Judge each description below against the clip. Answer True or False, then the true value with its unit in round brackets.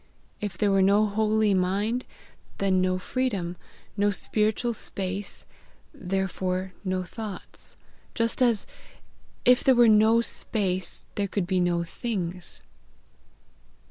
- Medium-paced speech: False (115 wpm)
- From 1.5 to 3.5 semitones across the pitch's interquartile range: True (2.9 semitones)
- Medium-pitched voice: False (200 Hz)